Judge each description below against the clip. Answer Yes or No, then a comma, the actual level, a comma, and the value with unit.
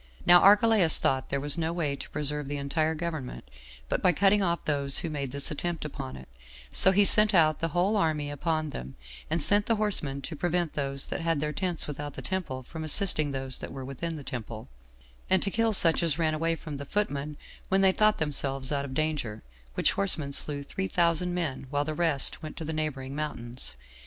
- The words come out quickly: Yes, fast, 210 wpm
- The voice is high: No, medium, 155 Hz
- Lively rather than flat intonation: No, average, 3.8 semitones